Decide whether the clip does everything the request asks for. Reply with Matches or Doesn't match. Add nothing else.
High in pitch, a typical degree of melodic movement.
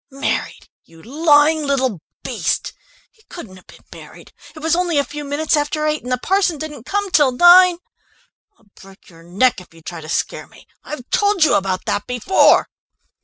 Doesn't match